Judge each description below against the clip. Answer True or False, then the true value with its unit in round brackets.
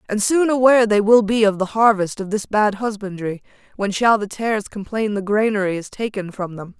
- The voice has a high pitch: True (210 Hz)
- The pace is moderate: False (210 wpm)